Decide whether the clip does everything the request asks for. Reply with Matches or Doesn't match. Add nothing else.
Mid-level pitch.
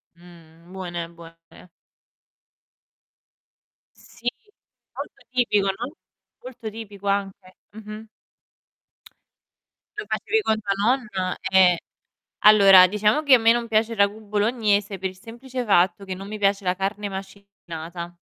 Doesn't match